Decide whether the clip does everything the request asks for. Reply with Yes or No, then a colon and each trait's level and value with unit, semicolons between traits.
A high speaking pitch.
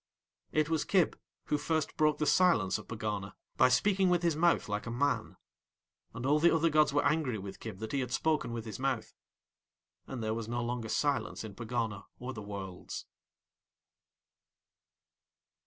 No: low, 125 Hz